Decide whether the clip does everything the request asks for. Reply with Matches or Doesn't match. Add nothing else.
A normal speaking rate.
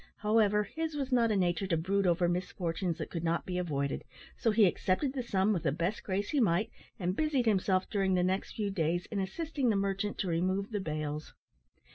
Doesn't match